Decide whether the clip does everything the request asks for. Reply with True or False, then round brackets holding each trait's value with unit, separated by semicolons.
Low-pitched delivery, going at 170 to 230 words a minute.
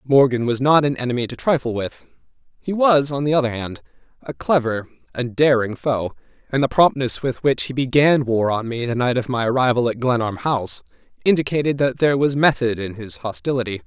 True (125 Hz; 195 wpm)